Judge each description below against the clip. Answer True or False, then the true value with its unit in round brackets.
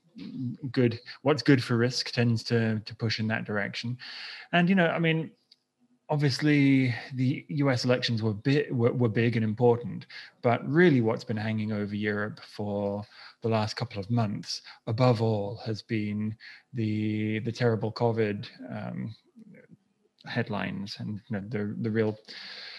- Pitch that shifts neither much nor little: True (3.7 semitones)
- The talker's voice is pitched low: True (115 Hz)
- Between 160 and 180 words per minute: False (150 wpm)